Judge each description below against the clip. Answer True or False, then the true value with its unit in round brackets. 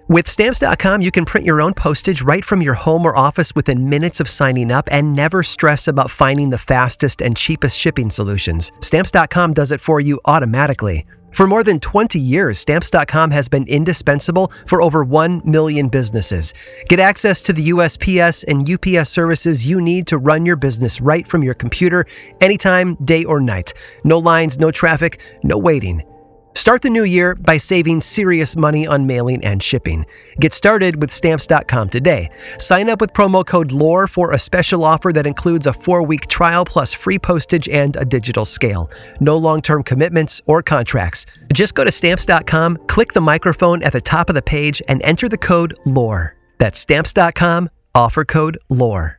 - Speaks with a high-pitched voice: False (155 Hz)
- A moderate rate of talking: True (180 wpm)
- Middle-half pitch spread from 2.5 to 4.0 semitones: False (4.4 semitones)